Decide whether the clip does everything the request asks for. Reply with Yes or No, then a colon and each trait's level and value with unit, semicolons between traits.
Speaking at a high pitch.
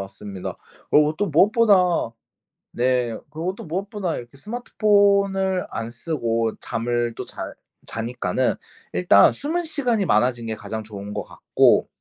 No: medium, 140 Hz